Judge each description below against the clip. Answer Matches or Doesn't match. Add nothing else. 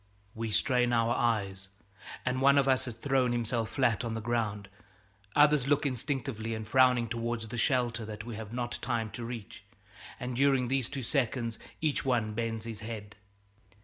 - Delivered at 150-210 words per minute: Matches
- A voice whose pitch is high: Doesn't match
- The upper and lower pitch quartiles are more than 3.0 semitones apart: Doesn't match